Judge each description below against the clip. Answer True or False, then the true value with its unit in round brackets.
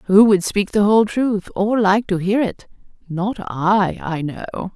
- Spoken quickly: False (175 wpm)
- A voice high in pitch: True (200 Hz)